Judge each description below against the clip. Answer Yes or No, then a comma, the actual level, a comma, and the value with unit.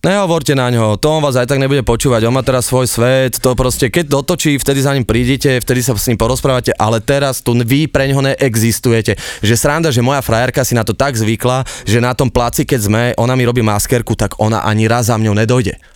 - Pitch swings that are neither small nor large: Yes, average, 3.1 semitones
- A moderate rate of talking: No, fast, 235 wpm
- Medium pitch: No, low, 125 Hz